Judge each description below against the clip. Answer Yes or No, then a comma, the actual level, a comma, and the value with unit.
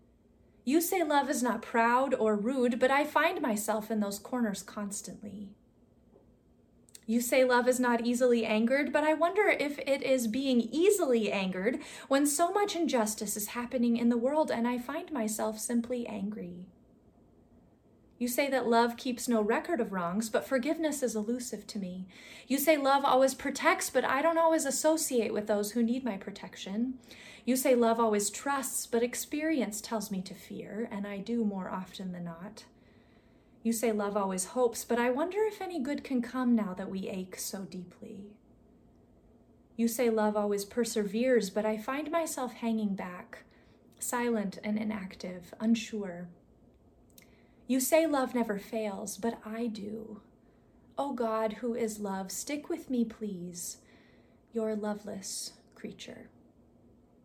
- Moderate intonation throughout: Yes, average, 3.8 semitones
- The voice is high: Yes, high, 235 Hz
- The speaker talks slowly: No, average, 155 wpm